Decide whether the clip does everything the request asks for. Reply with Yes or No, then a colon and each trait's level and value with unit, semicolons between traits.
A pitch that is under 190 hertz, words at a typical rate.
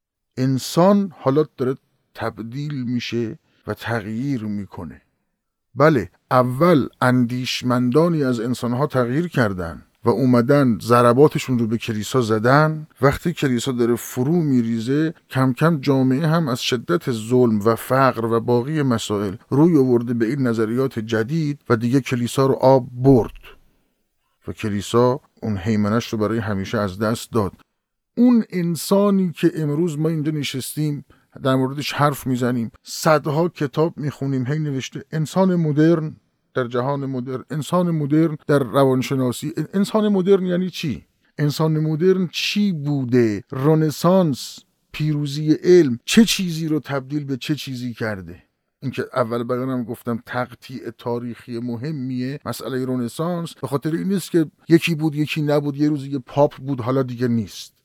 Yes: low, 135 Hz; average, 135 wpm